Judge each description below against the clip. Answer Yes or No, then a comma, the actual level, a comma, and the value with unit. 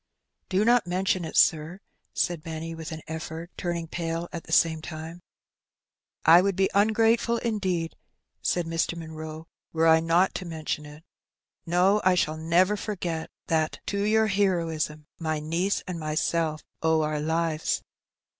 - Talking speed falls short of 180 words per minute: Yes, average, 160 wpm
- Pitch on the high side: No, medium, 165 Hz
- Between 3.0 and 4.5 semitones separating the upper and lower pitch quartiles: No, narrow, 2.6 semitones